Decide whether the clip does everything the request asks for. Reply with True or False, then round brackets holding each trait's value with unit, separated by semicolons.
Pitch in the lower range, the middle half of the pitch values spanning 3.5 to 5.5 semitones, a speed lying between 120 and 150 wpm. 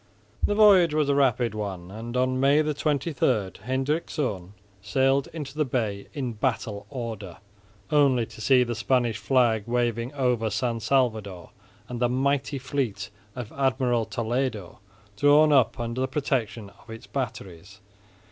True (125 Hz; 3.8 semitones; 140 wpm)